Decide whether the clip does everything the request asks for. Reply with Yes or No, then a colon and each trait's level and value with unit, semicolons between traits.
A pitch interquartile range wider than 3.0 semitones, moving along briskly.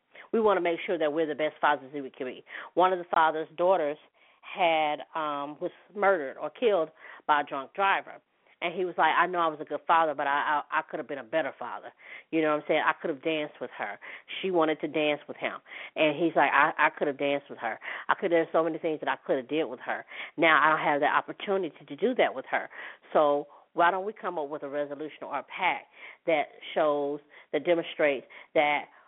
No: narrow, 2.6 semitones; fast, 245 wpm